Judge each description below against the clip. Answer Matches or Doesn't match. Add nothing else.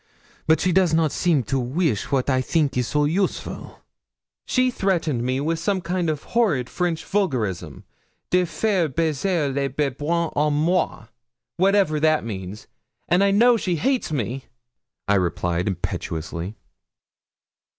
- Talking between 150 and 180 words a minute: Doesn't match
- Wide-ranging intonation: Matches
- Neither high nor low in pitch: Matches